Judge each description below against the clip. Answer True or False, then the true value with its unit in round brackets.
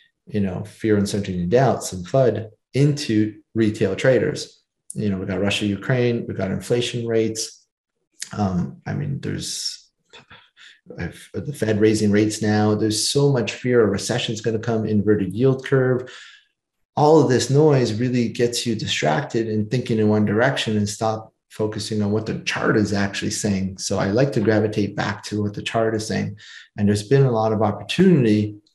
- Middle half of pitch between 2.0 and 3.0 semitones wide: True (2.7 semitones)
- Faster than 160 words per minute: True (175 wpm)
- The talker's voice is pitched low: True (110 Hz)